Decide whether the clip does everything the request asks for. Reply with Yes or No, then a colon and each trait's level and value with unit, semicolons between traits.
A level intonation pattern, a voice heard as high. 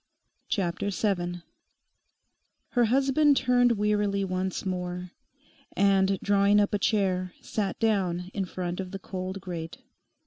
Yes: narrow, 2.3 semitones; high, 195 Hz